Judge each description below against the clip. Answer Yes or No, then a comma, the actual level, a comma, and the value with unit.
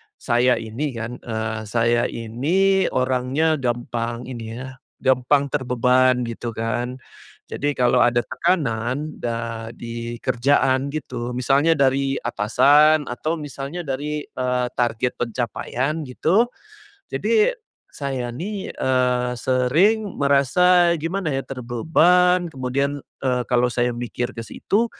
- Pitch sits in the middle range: No, low, 130 Hz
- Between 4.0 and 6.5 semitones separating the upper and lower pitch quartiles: No, average, 3.6 semitones